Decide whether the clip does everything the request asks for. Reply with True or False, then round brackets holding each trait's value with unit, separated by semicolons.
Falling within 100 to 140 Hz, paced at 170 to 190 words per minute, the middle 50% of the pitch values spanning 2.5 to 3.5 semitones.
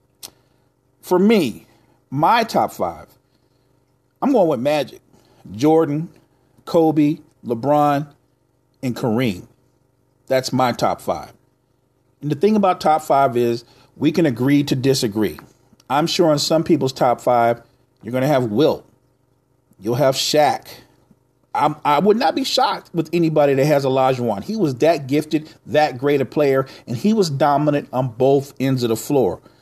False (135 Hz; 150 wpm; 2.8 semitones)